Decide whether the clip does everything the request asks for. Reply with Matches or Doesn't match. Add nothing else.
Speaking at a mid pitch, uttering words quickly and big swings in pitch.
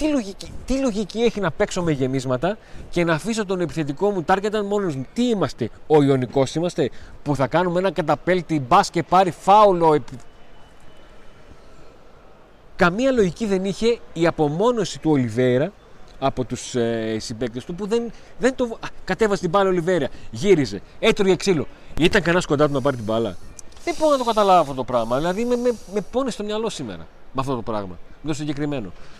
Matches